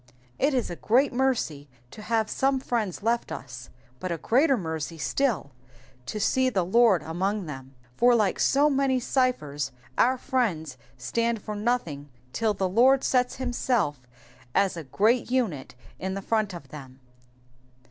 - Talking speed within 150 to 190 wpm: Yes, average, 155 wpm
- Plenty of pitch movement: Yes, wide, 7.5 semitones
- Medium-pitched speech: No, high, 215 Hz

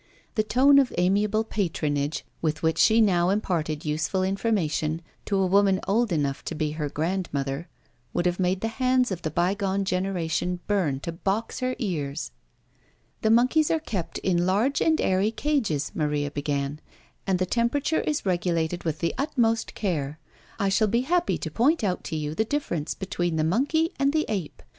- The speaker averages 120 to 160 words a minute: No, average, 175 wpm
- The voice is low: No, medium, 185 Hz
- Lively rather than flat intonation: Yes, wide, 5.8 semitones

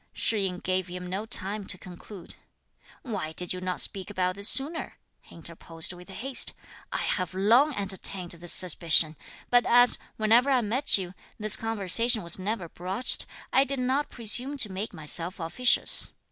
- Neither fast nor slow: Yes, average, 165 wpm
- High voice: Yes, high, 195 Hz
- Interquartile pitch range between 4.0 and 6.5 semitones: Yes, average, 4.7 semitones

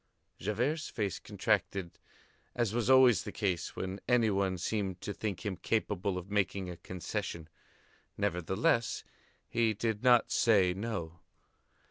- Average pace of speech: No, slow, 130 wpm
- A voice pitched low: Yes, low, 100 Hz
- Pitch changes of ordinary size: Yes, average, 3.5 semitones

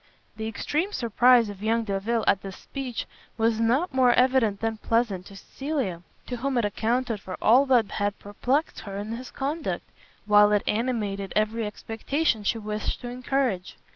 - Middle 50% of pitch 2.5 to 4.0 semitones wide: Yes, average, 3.6 semitones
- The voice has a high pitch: Yes, high, 225 Hz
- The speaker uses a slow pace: No, average, 170 wpm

